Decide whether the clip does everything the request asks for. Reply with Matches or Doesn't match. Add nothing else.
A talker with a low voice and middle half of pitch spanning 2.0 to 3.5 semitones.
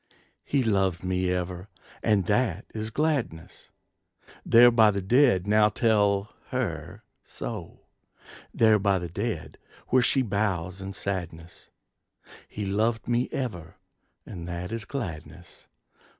Doesn't match